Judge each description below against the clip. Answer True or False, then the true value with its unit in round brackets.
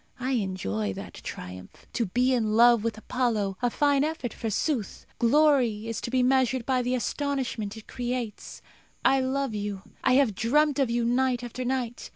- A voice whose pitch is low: False (245 Hz)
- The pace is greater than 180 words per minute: False (175 wpm)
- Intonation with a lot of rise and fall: False (3.2 semitones)